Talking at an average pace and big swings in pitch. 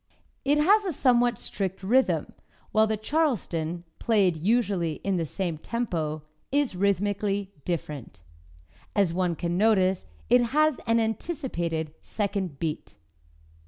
No: slow, 125 wpm; wide, 5.8 semitones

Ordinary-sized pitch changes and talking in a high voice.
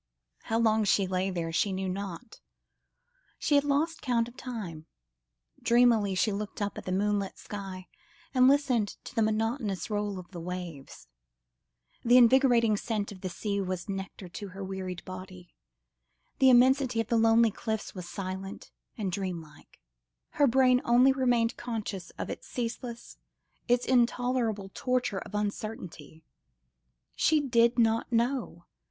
Yes: average, 4.3 semitones; high, 215 Hz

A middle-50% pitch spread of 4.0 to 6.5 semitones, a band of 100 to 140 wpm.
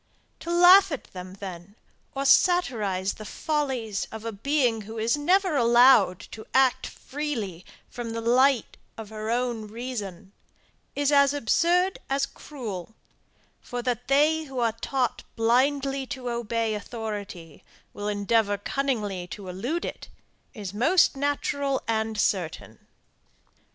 Yes: average, 4.8 semitones; slow, 135 wpm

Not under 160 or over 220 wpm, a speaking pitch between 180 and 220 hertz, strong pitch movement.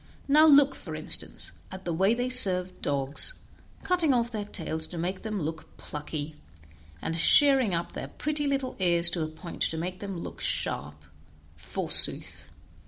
Yes: average, 170 wpm; medium, 185 Hz; wide, 7.8 semitones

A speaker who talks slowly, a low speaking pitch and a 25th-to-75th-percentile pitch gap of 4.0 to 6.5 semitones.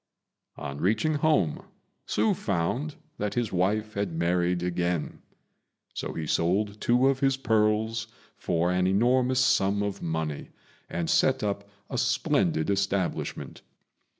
Yes: slow, 125 wpm; low, 100 Hz; average, 4.4 semitones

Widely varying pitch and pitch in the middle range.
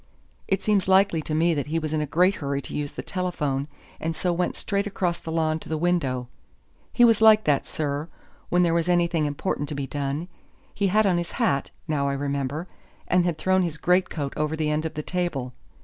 No: average, 3.6 semitones; medium, 160 Hz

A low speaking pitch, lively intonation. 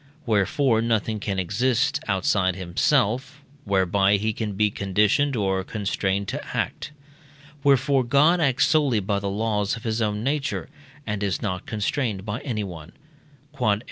No: low, 105 Hz; average, 4.5 semitones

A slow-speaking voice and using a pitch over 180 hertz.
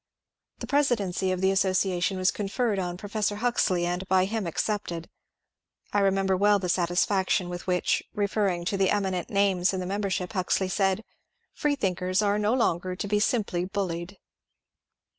No: average, 160 wpm; high, 190 Hz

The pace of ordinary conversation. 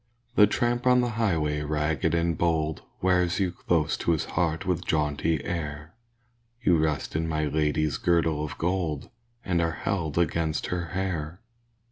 Yes: average, 155 wpm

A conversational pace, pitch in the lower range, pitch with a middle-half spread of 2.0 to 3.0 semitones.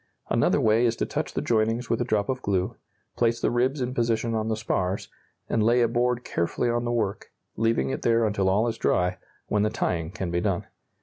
No: fast, 225 wpm; low, 115 Hz; narrow, 2.5 semitones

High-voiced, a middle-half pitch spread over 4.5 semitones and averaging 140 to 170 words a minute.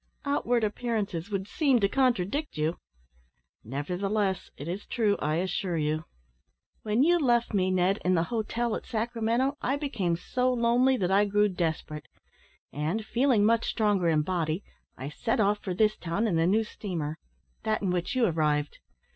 Yes: high, 205 Hz; average, 5.2 semitones; average, 165 wpm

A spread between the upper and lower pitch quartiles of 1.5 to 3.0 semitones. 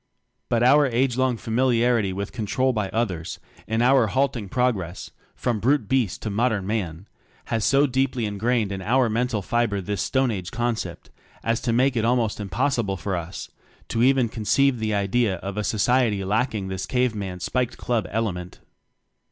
No: average, 3.9 semitones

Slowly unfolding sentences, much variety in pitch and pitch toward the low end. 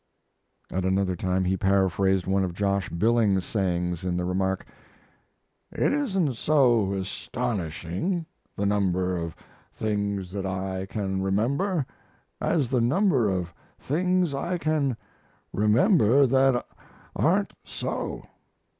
Yes: slow, 115 wpm; wide, 6.0 semitones; low, 100 Hz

